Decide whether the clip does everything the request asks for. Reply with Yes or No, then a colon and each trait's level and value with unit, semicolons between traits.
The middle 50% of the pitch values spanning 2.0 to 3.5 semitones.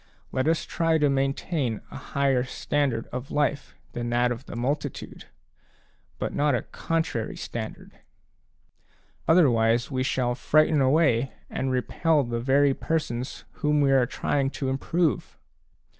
Yes: average, 3.2 semitones